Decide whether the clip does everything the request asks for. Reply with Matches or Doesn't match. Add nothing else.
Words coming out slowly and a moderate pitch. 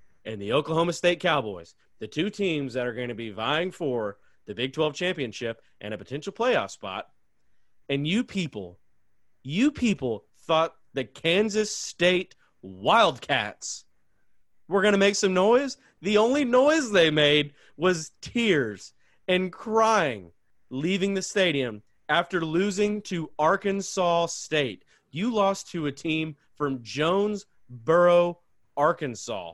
Matches